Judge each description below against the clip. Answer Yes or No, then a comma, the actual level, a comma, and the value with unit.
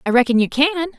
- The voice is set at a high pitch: Yes, very high, 280 Hz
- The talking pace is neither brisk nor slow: No, fast, 245 wpm